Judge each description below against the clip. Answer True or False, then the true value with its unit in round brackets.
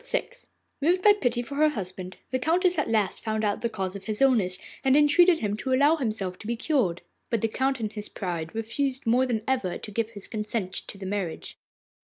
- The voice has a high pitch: True (225 Hz)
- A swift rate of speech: True (220 wpm)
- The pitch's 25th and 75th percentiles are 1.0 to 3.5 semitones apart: False (5.1 semitones)